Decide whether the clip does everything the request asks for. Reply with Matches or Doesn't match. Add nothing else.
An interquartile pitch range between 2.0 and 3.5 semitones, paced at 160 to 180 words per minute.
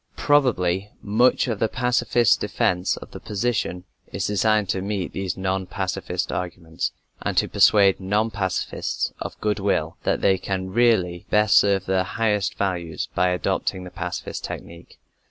Doesn't match